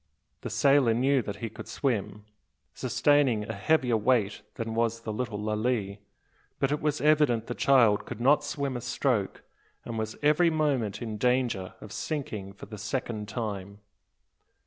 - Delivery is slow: No, average, 160 wpm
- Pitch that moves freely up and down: No, average, 4.5 semitones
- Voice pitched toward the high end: No, low, 120 Hz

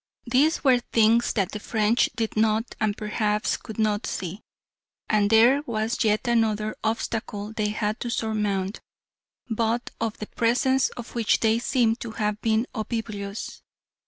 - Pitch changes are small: Yes, narrow, 1.7 semitones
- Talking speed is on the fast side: No, average, 150 wpm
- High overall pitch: Yes, high, 220 Hz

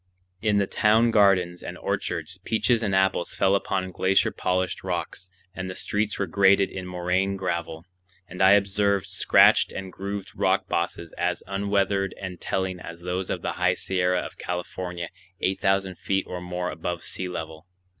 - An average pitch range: No, narrow, 1.6 semitones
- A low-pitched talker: Yes, very low, 95 Hz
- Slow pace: No, average, 165 wpm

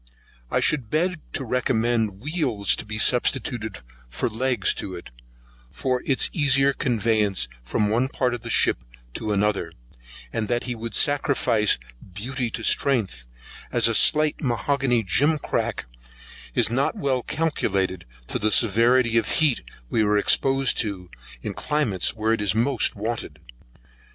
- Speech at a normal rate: Yes, average, 150 wpm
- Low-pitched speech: Yes, low, 115 Hz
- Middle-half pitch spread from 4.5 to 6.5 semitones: No, average, 4.1 semitones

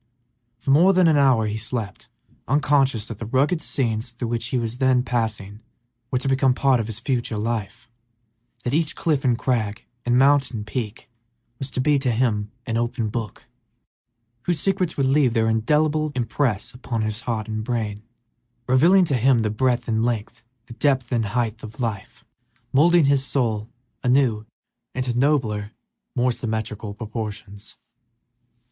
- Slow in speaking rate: No, average, 160 wpm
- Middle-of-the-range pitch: No, low, 120 Hz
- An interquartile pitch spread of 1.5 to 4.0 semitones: Yes, average, 3.5 semitones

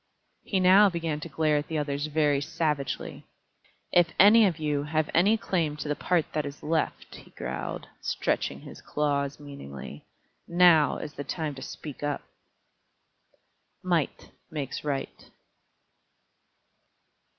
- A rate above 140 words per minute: No, slow, 135 wpm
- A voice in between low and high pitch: Yes, medium, 150 Hz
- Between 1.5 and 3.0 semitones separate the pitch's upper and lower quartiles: Yes, narrow, 2.6 semitones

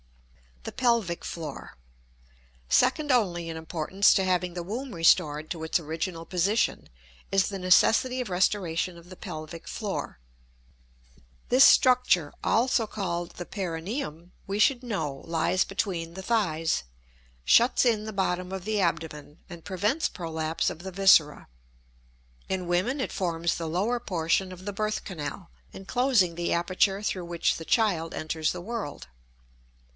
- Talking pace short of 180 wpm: Yes, average, 145 wpm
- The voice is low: No, medium, 180 Hz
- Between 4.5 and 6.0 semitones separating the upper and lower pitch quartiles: No, average, 4.0 semitones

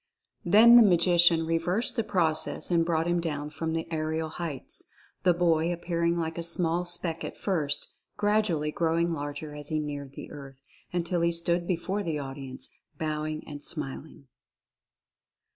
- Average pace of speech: Yes, average, 160 wpm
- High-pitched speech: No, medium, 165 Hz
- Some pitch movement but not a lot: No, narrow, 2.2 semitones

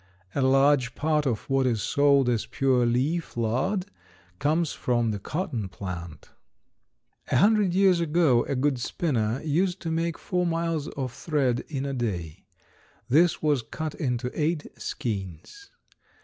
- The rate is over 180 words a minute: No, average, 145 wpm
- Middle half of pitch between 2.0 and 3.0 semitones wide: No, wide, 5.4 semitones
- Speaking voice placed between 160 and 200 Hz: No, medium, 140 Hz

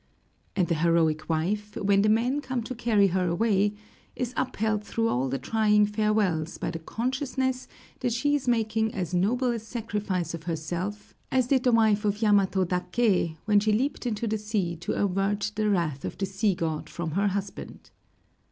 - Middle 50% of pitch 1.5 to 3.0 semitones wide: No, average, 4.0 semitones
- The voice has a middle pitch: No, high, 210 Hz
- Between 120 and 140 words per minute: No, average, 180 wpm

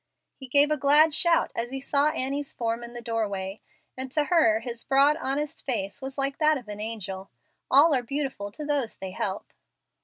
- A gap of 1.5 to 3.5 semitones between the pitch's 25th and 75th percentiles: No, average, 4.3 semitones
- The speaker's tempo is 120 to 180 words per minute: No, average, 195 wpm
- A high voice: Yes, very high, 265 Hz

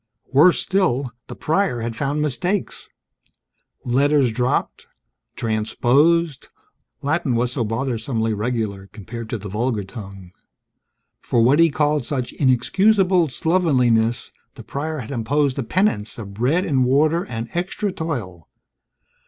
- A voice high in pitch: No, low, 130 Hz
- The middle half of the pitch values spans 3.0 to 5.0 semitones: No, wide, 5.6 semitones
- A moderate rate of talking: No, slow, 125 wpm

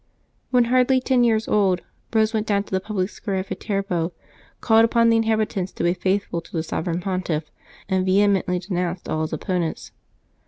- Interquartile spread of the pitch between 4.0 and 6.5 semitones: No, average, 3.6 semitones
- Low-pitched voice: No, high, 195 Hz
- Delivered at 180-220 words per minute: Yes, average, 185 wpm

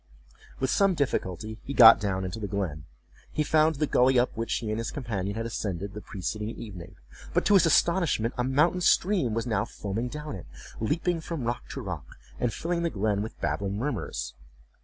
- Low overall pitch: Yes, low, 115 Hz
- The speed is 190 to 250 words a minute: Yes, average, 195 wpm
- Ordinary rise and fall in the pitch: No, wide, 6.6 semitones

